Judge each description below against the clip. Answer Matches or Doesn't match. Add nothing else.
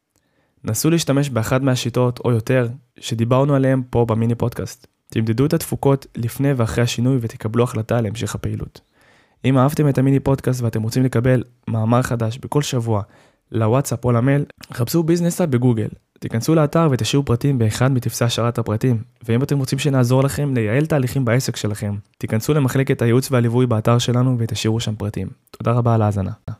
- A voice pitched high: Doesn't match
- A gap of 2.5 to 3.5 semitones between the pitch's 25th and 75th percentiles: Matches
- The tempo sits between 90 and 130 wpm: Doesn't match